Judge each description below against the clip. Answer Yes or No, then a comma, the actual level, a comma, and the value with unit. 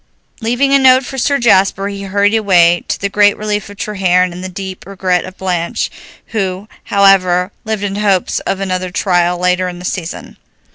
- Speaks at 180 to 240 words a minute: Yes, average, 185 wpm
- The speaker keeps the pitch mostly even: Yes, narrow, 2.2 semitones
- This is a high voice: Yes, high, 195 Hz